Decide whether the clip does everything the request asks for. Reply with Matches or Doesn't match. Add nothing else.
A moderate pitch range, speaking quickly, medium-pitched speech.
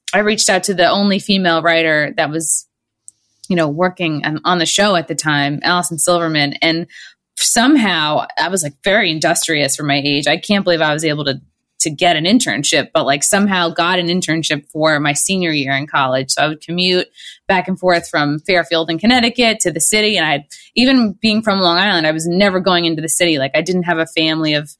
Matches